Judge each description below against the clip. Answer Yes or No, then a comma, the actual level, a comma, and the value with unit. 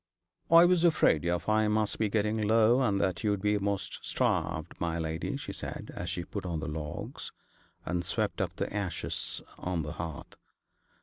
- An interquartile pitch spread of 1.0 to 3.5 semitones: No, average, 4.2 semitones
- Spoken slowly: No, average, 180 wpm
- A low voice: Yes, low, 100 Hz